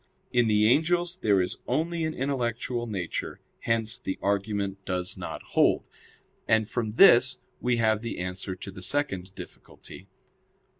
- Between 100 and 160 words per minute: Yes, average, 145 wpm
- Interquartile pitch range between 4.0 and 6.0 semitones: Yes, average, 4.3 semitones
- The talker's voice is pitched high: No, low, 110 Hz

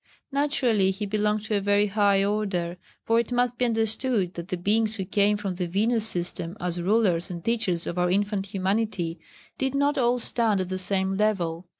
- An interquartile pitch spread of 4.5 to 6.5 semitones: No, average, 3.3 semitones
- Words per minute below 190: No, average, 195 wpm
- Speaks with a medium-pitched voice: No, high, 205 Hz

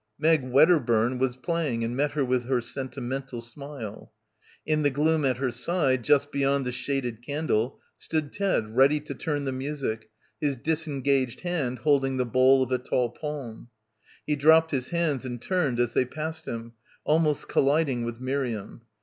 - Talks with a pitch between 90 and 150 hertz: Yes, low, 135 Hz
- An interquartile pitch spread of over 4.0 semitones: No, average, 3.4 semitones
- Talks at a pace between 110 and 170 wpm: Yes, average, 165 wpm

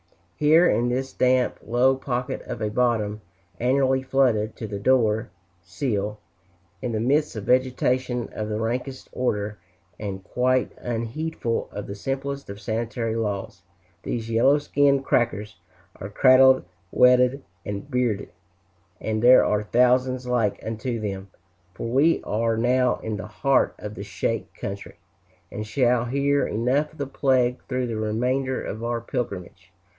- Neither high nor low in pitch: No, low, 120 Hz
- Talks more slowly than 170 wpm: Yes, average, 145 wpm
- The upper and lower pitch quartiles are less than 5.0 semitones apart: Yes, average, 3.3 semitones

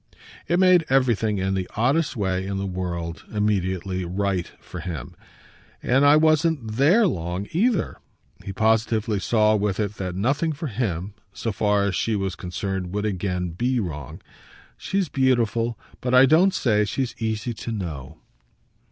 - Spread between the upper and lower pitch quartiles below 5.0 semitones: No, wide, 5.4 semitones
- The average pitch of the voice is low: Yes, low, 105 Hz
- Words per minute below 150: No, average, 155 wpm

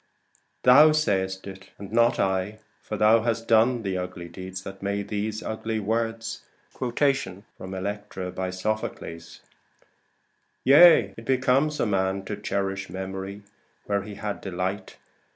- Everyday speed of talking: No, slow, 125 wpm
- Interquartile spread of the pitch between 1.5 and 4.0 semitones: Yes, average, 3.1 semitones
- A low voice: Yes, low, 100 Hz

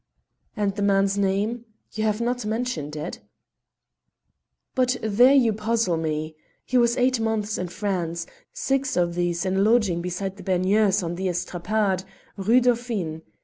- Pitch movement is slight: No, average, 4.5 semitones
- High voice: Yes, high, 200 Hz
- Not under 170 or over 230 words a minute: No, average, 150 wpm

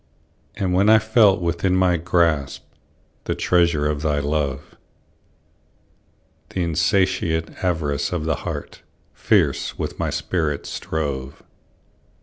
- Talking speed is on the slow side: Yes, slow, 110 wpm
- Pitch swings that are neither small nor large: Yes, average, 3.7 semitones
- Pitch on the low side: Yes, very low, 85 Hz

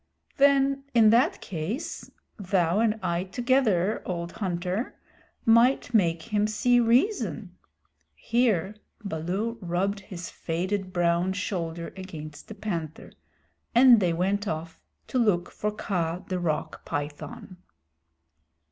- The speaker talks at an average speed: No, slow, 115 wpm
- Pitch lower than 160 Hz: No, high, 190 Hz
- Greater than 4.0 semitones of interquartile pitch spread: Yes, average, 4.9 semitones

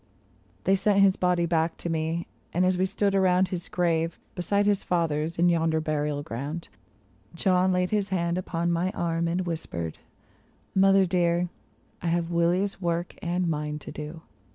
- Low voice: No, medium, 170 Hz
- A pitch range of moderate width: No, narrow, 2.0 semitones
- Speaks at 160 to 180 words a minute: Yes, average, 170 wpm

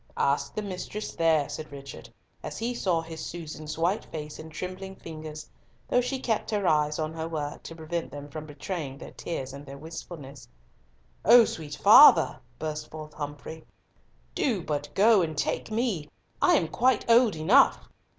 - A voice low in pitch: No, medium, 160 Hz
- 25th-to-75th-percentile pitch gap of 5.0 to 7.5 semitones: No, average, 4.3 semitones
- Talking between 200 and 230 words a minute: No, average, 170 wpm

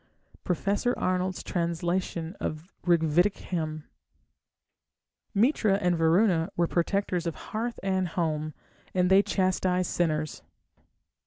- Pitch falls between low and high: Yes, medium, 180 Hz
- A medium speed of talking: No, slow, 100 wpm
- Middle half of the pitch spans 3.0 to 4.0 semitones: No, narrow, 2.6 semitones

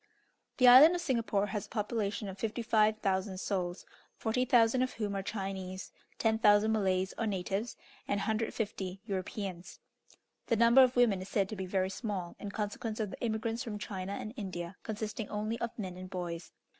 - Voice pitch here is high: Yes, high, 210 Hz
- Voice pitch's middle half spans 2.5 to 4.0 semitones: Yes, average, 2.9 semitones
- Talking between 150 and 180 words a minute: Yes, average, 170 wpm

